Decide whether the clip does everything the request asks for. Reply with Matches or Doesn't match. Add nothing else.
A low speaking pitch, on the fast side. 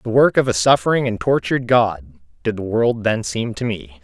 Matches